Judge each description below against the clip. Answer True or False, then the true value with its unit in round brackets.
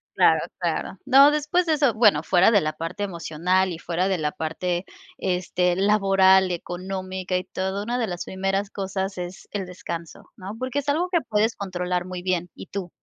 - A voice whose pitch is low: False (190 Hz)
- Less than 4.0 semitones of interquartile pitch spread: True (2.6 semitones)